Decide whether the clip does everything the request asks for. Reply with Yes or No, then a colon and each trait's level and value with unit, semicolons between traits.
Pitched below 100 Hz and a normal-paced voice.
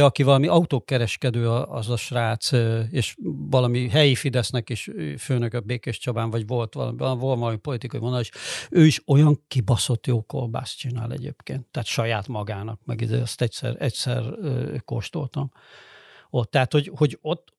No: low, 125 Hz; average, 145 wpm